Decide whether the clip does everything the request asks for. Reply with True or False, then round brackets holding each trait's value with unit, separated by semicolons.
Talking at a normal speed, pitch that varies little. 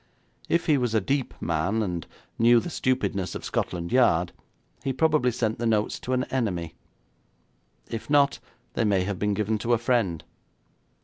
False (170 wpm; 4.8 semitones)